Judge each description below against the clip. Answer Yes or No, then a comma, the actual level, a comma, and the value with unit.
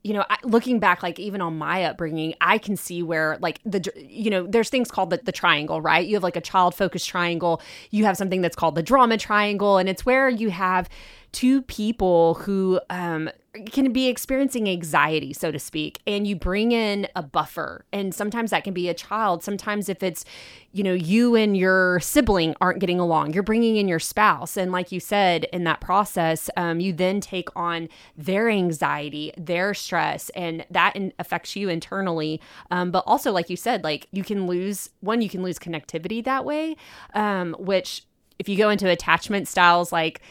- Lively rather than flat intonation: No, average, 3.3 semitones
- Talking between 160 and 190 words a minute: No, average, 200 wpm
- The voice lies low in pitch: No, medium, 185 Hz